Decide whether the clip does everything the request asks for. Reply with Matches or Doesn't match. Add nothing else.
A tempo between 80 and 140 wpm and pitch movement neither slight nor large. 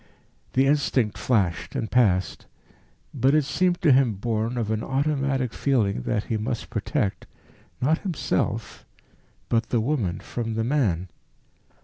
Matches